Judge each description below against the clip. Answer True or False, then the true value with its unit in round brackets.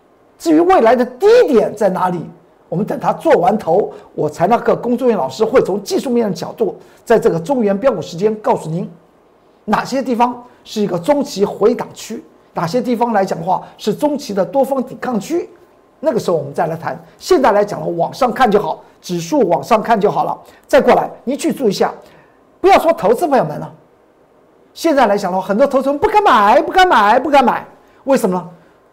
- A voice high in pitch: True (240 Hz)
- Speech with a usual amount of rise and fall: False (6.1 semitones)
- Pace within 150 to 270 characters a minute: False (305 characters per minute)